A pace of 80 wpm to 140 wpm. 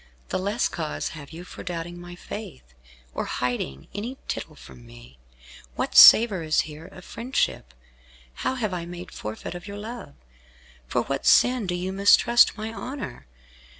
No: average, 160 wpm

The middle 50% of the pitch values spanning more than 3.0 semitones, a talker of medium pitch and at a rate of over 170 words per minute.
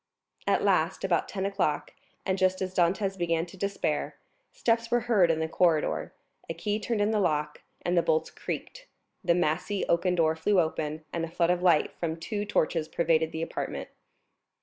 Yes: average, 3.5 semitones; medium, 175 Hz; average, 180 wpm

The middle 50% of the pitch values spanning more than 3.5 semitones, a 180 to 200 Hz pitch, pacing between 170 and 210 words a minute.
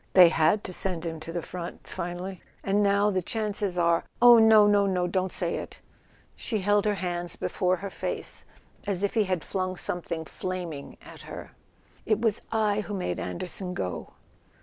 No: average, 2.7 semitones; medium, 185 Hz; average, 180 wpm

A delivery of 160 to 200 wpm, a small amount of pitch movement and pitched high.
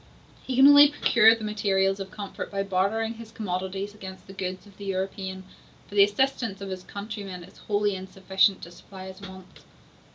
Yes: average, 185 wpm; narrow, 2.0 semitones; high, 195 Hz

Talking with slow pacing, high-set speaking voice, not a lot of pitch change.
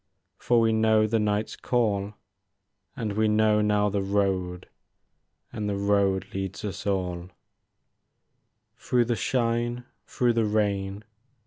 No: slow, 125 wpm; low, 105 Hz; narrow, 2.1 semitones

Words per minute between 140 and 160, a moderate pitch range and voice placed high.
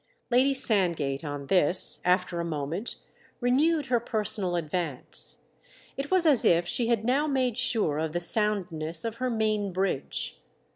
No: average, 150 wpm; wide, 6.6 semitones; high, 205 Hz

